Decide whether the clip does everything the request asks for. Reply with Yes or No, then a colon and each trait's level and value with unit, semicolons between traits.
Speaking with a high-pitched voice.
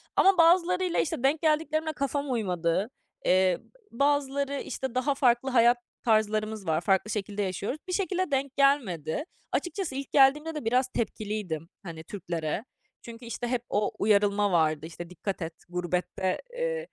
Yes: high, 235 Hz